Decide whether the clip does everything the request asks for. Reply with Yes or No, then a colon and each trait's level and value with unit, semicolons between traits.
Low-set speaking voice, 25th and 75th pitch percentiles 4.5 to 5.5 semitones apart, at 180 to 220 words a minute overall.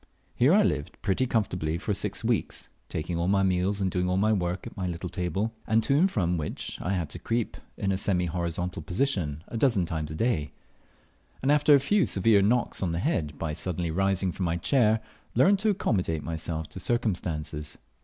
Yes: very low, 95 Hz; average, 5.0 semitones; average, 200 wpm